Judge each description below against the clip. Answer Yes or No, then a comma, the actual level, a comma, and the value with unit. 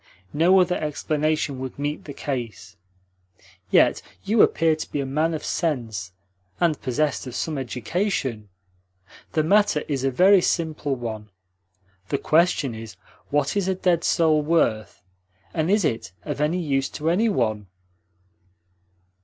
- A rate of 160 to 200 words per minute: No, average, 145 wpm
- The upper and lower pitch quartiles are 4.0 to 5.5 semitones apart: Yes, average, 4.6 semitones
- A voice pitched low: No, medium, 150 Hz